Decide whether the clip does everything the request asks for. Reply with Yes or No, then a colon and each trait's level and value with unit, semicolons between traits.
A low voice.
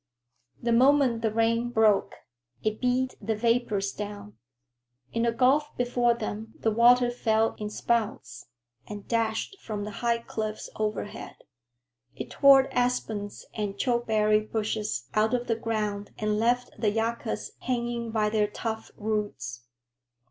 No: high, 225 Hz